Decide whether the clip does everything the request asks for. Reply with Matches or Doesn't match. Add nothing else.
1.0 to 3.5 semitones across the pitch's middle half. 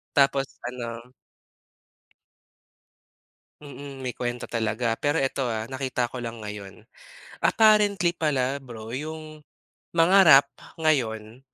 Doesn't match